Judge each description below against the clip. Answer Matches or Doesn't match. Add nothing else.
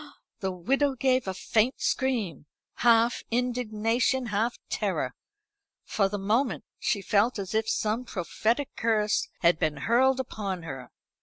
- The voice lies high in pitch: Matches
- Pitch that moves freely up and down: Doesn't match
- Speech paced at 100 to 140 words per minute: Matches